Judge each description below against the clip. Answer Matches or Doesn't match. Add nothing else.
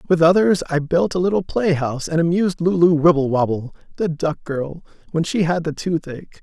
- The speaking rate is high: Doesn't match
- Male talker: Matches